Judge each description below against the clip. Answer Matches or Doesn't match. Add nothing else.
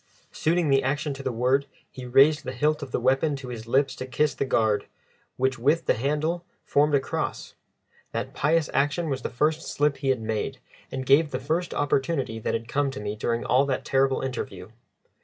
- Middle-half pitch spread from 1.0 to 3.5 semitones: Matches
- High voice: Doesn't match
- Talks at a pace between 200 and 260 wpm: Matches